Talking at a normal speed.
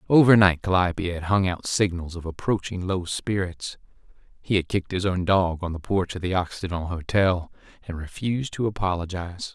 Yes: average, 175 wpm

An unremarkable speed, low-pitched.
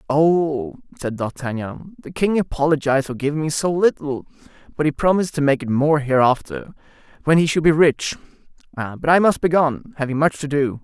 No: average, 185 wpm; medium, 150 Hz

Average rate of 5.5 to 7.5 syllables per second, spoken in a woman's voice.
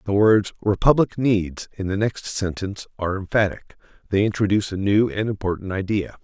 No: 5.7 syllables/s; male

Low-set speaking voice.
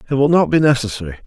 Yes: low, 125 Hz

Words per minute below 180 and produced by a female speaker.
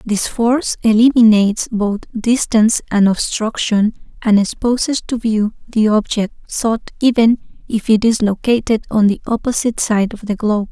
Yes: average, 145 wpm; female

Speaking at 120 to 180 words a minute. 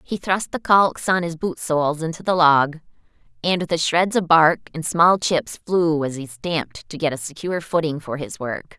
No: fast, 205 wpm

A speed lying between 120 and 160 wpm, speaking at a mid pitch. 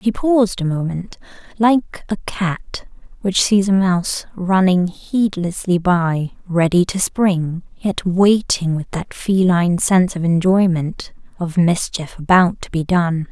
Yes: average, 140 wpm; medium, 180 Hz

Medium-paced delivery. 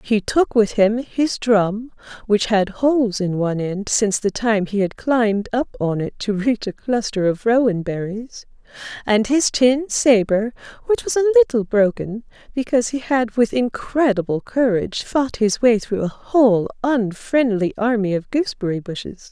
Yes: average, 170 wpm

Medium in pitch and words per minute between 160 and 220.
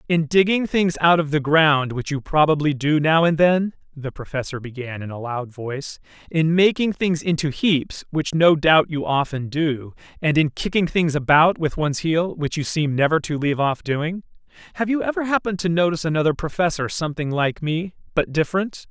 Yes: medium, 155 Hz; average, 185 wpm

